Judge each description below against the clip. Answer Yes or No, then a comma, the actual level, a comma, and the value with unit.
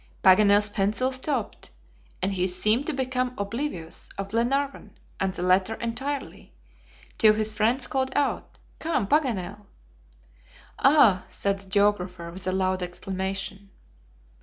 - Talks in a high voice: Yes, high, 205 Hz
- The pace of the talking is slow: Yes, slow, 125 wpm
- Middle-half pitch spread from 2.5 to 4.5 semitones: No, average, 5.1 semitones